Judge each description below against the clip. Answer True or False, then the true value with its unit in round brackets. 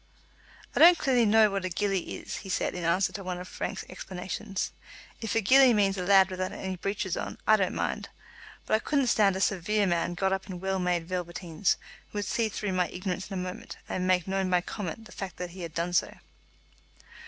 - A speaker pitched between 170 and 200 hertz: True (190 Hz)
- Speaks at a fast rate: True (220 wpm)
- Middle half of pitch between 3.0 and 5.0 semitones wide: False (2.4 semitones)